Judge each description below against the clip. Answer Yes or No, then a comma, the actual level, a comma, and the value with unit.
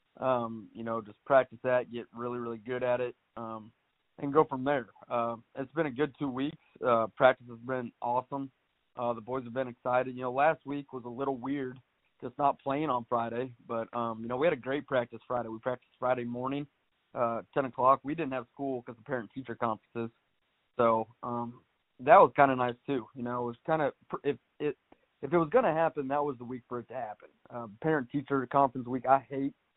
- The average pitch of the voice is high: No, low, 125 Hz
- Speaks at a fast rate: Yes, fast, 230 wpm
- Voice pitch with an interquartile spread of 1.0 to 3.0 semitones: Yes, narrow, 2.6 semitones